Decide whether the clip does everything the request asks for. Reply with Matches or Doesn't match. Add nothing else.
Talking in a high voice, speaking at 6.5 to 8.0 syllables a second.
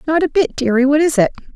Matches